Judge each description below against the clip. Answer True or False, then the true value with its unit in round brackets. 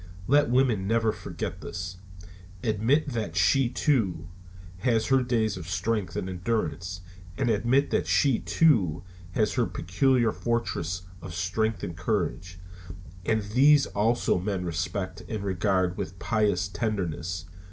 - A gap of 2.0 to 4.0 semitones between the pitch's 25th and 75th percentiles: False (4.6 semitones)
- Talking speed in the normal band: False (130 wpm)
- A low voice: True (105 Hz)